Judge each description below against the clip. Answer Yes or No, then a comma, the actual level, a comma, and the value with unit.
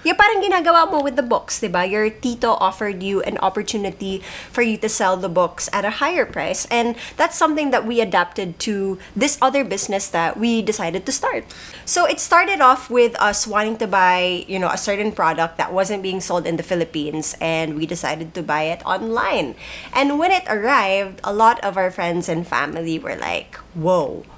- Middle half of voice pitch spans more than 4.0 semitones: Yes, average, 5.3 semitones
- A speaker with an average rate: Yes, average, 195 wpm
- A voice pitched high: Yes, high, 200 Hz